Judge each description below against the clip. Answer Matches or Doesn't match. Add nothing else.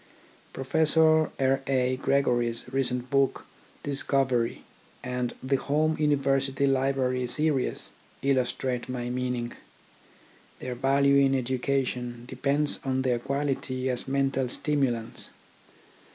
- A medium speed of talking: Doesn't match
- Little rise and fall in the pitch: Matches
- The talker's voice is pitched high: Doesn't match